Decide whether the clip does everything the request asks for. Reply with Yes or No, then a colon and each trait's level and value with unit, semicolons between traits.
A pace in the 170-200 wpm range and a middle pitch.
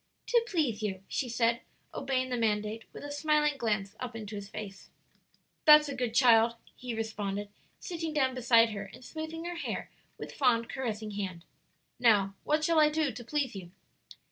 No: average, 175 wpm; high, 235 Hz